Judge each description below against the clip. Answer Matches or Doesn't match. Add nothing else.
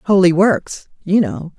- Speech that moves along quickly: Doesn't match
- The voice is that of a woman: Matches